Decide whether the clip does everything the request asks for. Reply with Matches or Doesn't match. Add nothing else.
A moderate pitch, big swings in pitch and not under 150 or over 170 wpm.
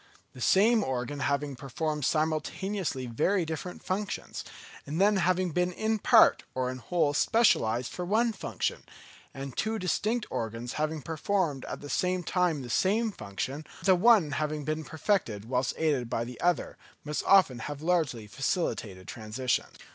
Matches